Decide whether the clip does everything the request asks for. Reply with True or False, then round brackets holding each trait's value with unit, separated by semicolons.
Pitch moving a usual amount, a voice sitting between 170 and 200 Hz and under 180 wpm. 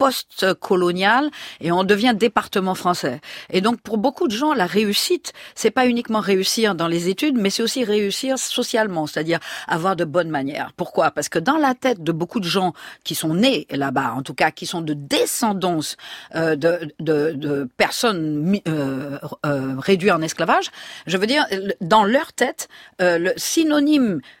False (6.6 semitones; 190 Hz; 165 wpm)